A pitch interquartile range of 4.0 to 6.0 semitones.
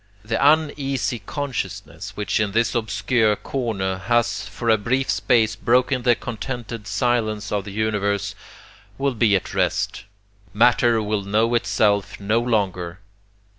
No: average, 2.9 semitones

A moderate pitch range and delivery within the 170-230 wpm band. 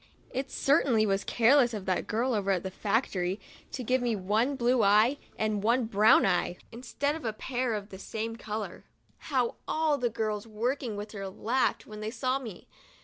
Yes: average, 3.6 semitones; average, 190 wpm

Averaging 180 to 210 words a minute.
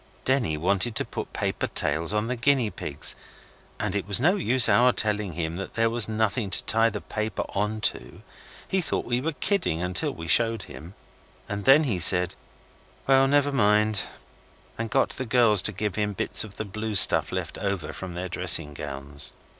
Yes: average, 185 wpm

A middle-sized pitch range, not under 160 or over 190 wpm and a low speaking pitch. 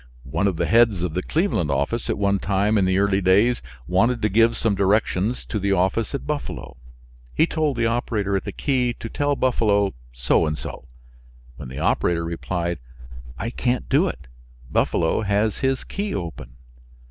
Yes: average, 4.7 semitones; average, 180 wpm; low, 100 Hz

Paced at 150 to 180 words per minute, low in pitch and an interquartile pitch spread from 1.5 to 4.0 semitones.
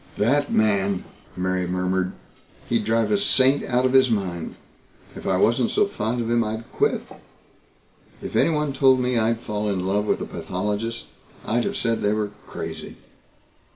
Yes: average, 165 wpm; low, 110 Hz; average, 3.6 semitones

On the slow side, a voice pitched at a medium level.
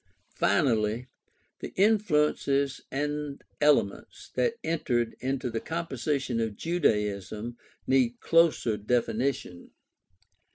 No: slow, 85 wpm; low, 130 Hz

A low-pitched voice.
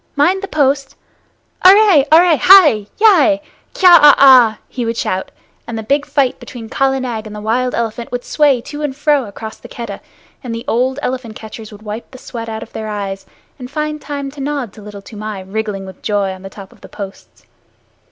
No: high, 245 Hz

